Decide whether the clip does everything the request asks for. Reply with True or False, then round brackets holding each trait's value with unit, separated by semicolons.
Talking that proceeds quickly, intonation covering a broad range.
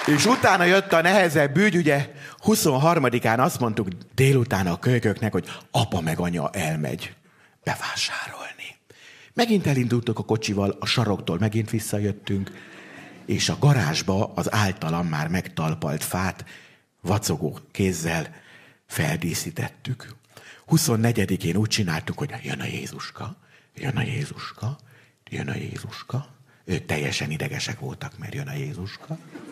False (120 wpm; 6.1 semitones)